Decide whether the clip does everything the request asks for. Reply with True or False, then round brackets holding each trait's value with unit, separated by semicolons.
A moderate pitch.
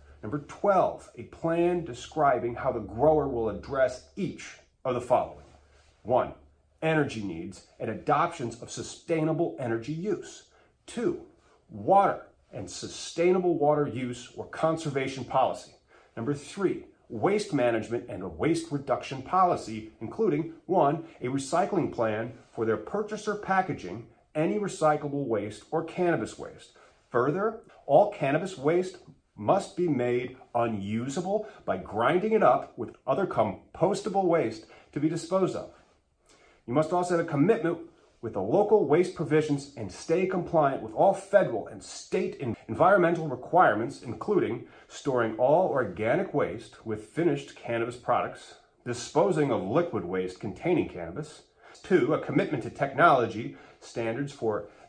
True (145 Hz)